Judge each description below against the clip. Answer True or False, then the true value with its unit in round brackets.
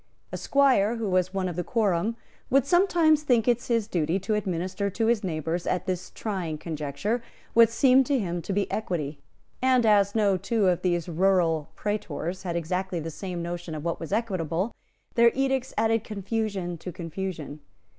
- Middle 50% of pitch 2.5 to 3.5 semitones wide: False (4.7 semitones)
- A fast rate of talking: False (175 wpm)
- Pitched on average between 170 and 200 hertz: True (190 Hz)